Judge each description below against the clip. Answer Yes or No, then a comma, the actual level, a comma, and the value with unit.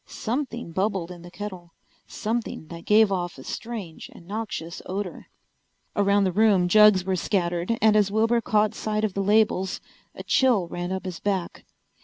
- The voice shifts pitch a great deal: No, average, 3.3 semitones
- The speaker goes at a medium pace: Yes, average, 170 wpm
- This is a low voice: No, high, 200 Hz